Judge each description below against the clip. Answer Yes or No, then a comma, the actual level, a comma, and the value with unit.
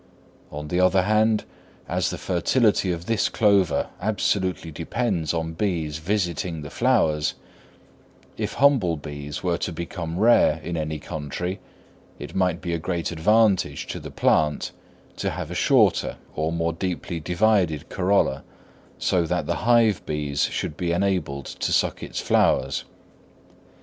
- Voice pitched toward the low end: Yes, very low, 85 Hz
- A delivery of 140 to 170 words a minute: Yes, average, 145 wpm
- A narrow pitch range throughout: No, average, 4.0 semitones